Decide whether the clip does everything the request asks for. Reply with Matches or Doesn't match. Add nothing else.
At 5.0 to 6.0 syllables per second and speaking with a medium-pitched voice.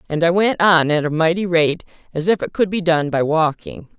Matches